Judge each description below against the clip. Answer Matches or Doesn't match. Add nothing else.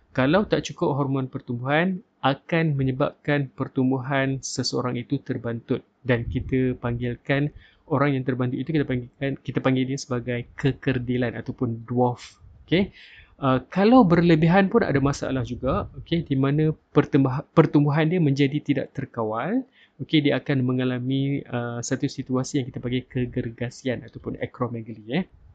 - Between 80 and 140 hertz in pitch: Matches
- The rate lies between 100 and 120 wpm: Doesn't match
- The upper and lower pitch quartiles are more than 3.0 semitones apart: Doesn't match